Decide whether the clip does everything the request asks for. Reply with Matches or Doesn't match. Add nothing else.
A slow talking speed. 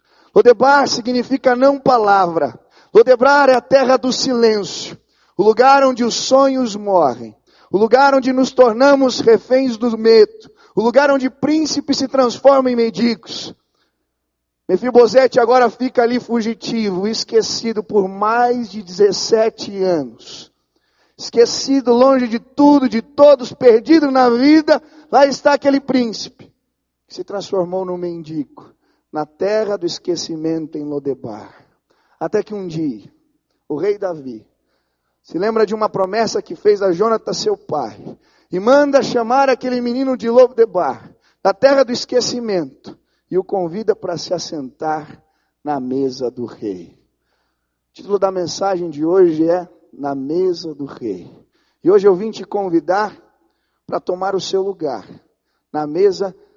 Doesn't match